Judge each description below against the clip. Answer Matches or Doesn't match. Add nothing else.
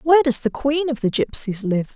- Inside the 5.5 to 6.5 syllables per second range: Doesn't match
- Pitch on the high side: Matches